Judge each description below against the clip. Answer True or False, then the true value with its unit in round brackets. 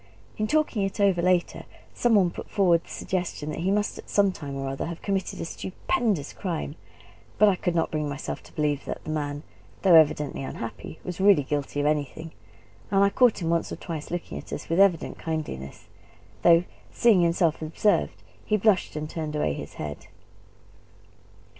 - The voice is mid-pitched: True (170 Hz)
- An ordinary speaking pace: True (185 wpm)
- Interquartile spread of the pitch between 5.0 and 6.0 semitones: False (4.5 semitones)